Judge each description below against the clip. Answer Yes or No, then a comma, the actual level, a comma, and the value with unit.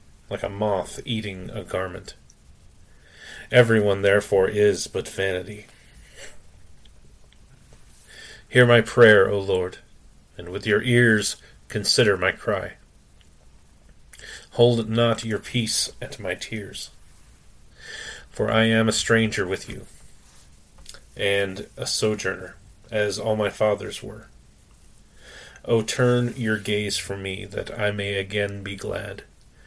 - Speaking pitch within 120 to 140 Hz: No, low, 105 Hz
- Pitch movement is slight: Yes, narrow, 2.3 semitones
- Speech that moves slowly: Yes, slow, 115 wpm